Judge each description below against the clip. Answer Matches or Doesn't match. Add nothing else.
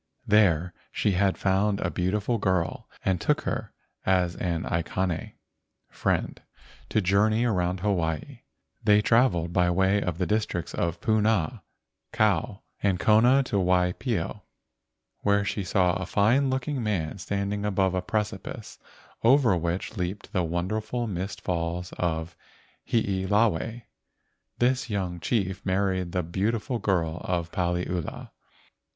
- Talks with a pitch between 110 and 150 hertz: Doesn't match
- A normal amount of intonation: Matches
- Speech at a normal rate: Doesn't match